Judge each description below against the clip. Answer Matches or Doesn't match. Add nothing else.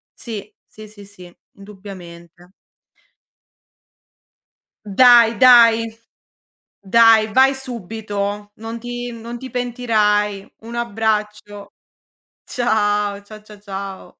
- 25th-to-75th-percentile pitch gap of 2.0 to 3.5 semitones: Matches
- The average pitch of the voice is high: Matches